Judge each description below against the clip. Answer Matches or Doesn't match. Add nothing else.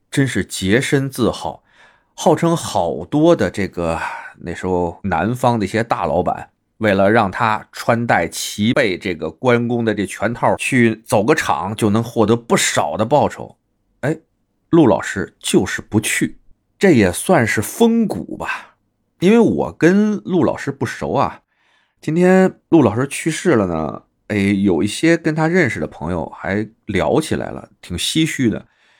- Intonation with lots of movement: Matches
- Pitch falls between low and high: Doesn't match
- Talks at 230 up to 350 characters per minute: Doesn't match